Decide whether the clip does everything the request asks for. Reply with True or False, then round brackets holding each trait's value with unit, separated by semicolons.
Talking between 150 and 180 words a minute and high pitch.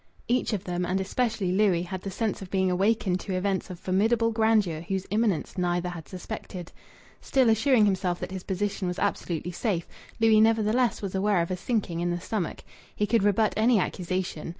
False (190 wpm; 195 Hz)